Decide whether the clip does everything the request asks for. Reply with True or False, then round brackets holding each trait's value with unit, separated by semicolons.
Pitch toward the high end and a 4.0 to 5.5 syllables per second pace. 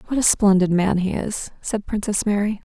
True (200 Hz; 5.1 syllables/s)